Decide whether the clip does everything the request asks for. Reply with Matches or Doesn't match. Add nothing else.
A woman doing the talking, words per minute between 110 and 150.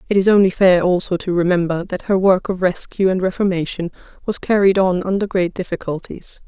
Doesn't match